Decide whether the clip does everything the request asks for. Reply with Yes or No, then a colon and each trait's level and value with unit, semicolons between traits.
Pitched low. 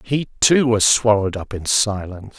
Yes: low, 110 Hz